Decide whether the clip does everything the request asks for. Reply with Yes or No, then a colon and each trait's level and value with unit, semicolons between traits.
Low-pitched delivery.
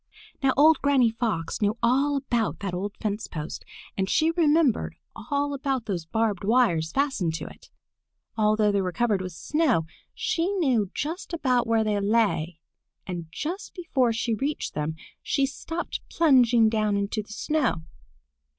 No: high, 230 Hz